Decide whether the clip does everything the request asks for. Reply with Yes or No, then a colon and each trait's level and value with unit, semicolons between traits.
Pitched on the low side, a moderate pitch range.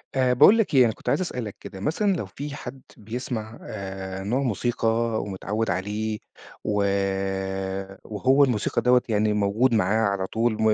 Yes: low, 110 Hz; average, 3.5 semitones